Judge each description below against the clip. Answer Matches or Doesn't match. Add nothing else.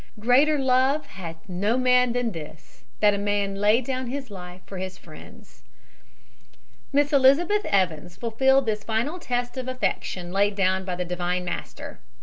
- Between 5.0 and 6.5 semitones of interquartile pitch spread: Matches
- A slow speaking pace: Doesn't match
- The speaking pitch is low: Doesn't match